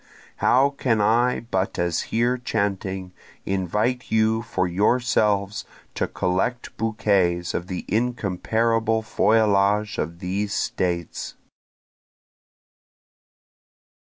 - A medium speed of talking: No, slow, 90 wpm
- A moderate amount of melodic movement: Yes, average, 3.4 semitones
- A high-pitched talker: No, low, 105 Hz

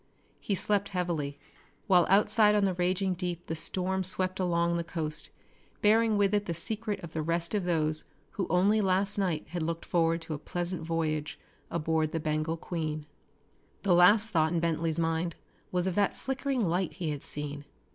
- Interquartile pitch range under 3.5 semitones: Yes, average, 3.0 semitones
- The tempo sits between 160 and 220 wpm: Yes, average, 185 wpm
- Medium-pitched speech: Yes, medium, 175 Hz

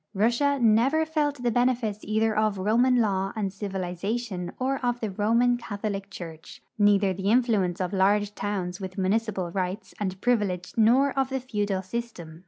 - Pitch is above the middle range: Yes, high, 210 Hz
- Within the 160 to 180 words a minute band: Yes, average, 170 wpm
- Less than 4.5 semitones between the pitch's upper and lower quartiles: Yes, average, 4.0 semitones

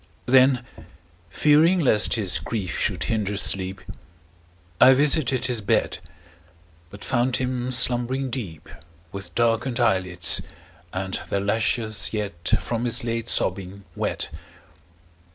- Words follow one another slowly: Yes, slow, 115 wpm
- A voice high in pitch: No, low, 115 Hz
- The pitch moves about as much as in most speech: Yes, average, 4.4 semitones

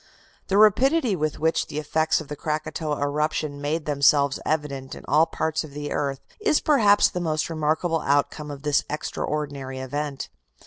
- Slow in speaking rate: No, average, 165 wpm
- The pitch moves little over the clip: Yes, narrow, 2.0 semitones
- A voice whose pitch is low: No, medium, 150 Hz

